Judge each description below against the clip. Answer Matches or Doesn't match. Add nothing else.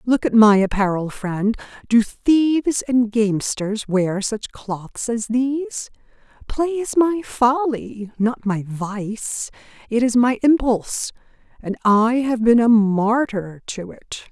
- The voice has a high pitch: Matches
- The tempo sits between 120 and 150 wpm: Matches